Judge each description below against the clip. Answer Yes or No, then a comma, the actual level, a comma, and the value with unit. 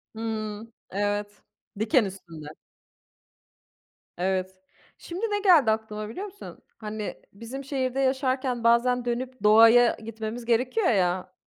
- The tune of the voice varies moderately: Yes, average, 3.6 semitones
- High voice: Yes, high, 230 Hz